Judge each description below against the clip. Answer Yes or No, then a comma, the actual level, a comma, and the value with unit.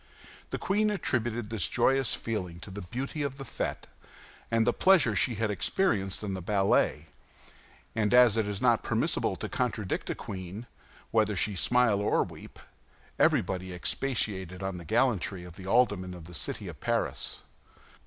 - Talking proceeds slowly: No, average, 165 wpm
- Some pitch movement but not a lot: Yes, average, 4.6 semitones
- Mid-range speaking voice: No, low, 105 Hz